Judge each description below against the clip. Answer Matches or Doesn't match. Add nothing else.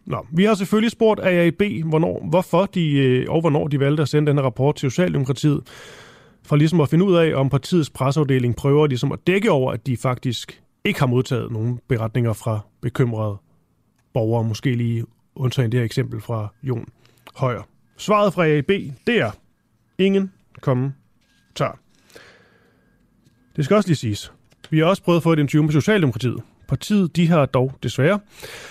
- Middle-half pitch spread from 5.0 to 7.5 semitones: Matches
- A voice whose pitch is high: Doesn't match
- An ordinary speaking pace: Matches